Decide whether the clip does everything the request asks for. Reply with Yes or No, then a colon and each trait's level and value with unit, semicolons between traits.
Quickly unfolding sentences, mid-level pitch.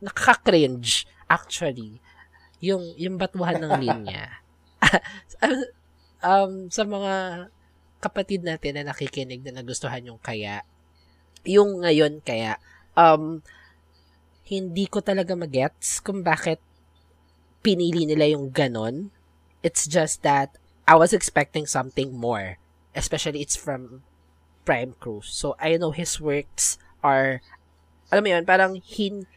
No: average, 115 wpm; medium, 145 Hz